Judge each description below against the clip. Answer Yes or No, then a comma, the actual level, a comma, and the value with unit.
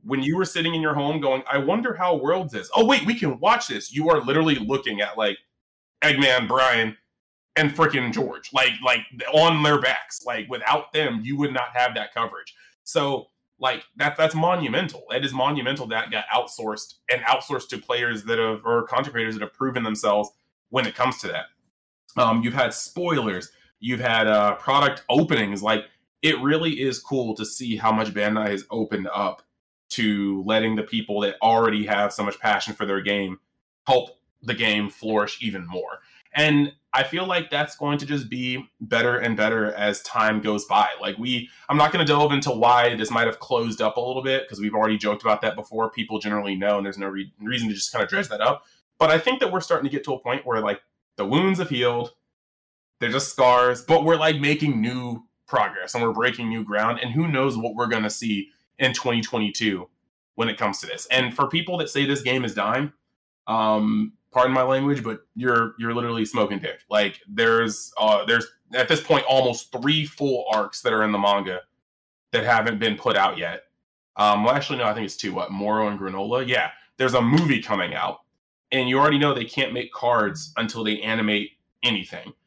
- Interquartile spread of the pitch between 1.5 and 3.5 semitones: No, average, 4.4 semitones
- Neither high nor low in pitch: No, low, 120 Hz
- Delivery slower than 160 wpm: No, fast, 205 wpm